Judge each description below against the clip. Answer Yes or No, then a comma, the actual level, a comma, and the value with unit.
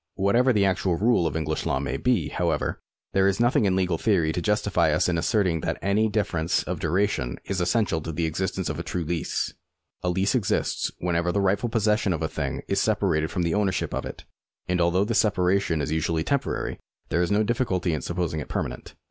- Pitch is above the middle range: No, very low, 90 Hz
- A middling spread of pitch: Yes, average, 3.9 semitones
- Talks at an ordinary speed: No, fast, 220 wpm